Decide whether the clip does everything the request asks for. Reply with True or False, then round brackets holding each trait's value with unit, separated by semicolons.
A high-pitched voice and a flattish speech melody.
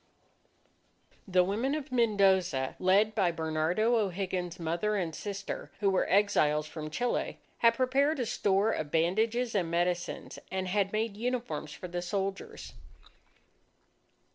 False (195 Hz; 4.2 semitones)